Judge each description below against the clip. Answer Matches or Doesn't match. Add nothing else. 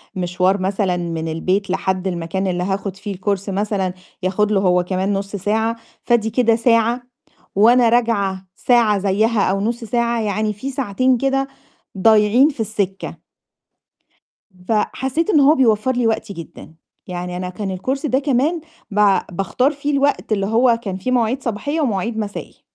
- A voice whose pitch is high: Matches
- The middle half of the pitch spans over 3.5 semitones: Matches